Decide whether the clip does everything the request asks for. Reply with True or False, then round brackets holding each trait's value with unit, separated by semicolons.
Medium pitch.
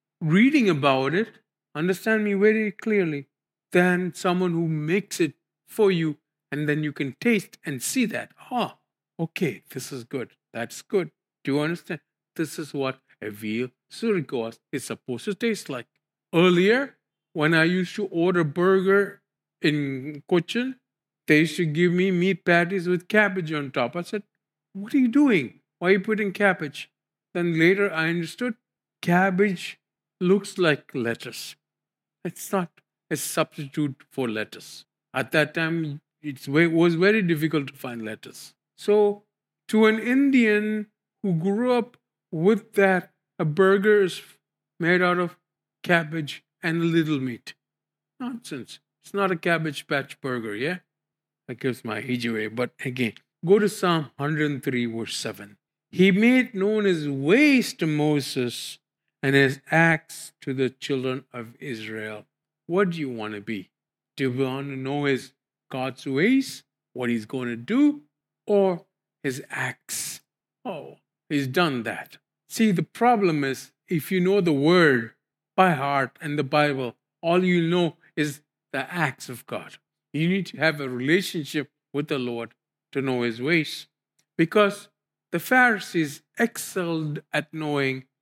True (160 Hz)